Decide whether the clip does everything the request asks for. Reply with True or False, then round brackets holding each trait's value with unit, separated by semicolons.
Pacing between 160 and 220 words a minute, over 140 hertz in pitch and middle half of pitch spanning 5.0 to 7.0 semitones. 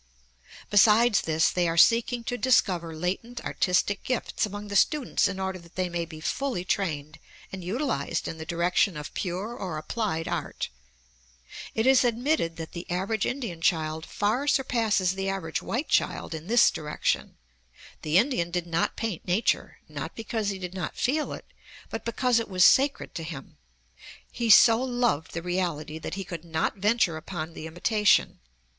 True (170 wpm; 190 Hz; 5.5 semitones)